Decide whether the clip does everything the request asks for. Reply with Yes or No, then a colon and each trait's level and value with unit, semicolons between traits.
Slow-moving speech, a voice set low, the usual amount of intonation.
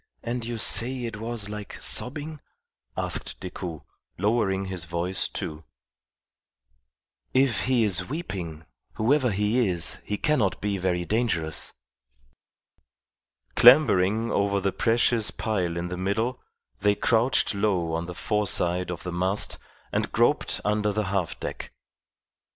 Yes: slow, 130 wpm; low, 105 Hz; average, 4.4 semitones